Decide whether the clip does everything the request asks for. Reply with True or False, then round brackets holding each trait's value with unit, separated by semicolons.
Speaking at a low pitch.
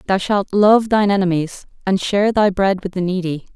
False (195 Hz)